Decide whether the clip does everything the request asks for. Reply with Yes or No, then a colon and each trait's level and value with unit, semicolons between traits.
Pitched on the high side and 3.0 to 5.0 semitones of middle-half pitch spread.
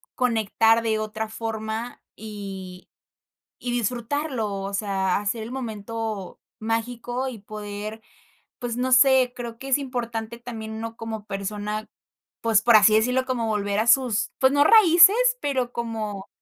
No: high, 225 Hz; narrow, 2.5 semitones